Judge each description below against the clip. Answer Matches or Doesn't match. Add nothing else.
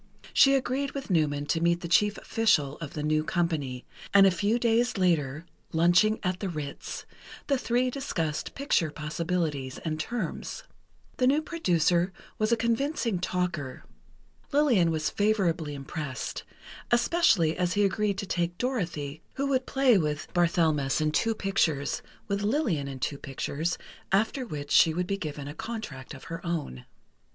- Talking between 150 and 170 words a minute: Matches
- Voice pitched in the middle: Matches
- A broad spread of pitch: Matches